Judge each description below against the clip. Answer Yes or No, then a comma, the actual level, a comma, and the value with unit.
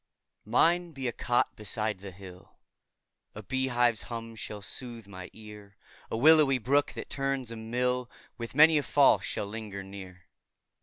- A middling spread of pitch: Yes, average, 4.3 semitones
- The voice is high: No, low, 115 Hz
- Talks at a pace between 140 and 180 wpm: Yes, average, 160 wpm